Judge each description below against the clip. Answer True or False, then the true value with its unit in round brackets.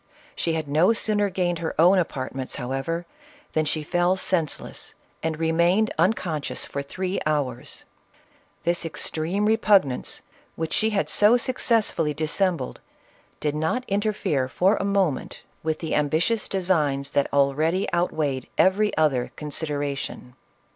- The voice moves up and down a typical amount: True (4.4 semitones)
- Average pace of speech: False (130 wpm)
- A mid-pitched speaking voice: True (165 Hz)